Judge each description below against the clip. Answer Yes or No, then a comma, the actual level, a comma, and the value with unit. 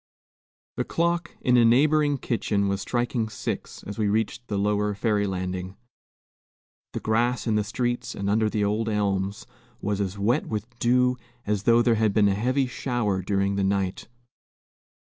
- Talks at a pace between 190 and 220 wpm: No, average, 165 wpm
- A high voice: No, low, 105 Hz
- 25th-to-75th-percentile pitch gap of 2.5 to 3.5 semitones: Yes, average, 3.2 semitones